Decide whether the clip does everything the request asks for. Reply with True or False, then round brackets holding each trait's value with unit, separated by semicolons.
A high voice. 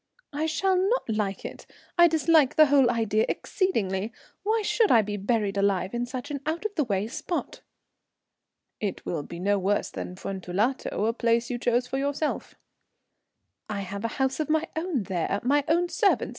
True (245 Hz)